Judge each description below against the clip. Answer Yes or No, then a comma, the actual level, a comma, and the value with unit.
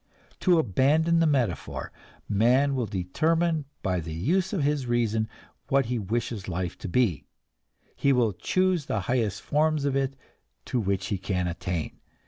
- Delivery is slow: No, average, 155 wpm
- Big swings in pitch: Yes, wide, 7.2 semitones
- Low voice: Yes, low, 120 Hz